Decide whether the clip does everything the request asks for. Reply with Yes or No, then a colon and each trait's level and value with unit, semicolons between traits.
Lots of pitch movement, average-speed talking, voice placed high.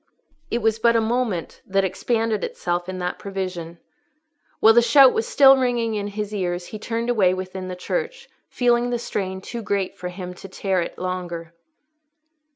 No: average, 4.2 semitones; average, 175 wpm; high, 200 Hz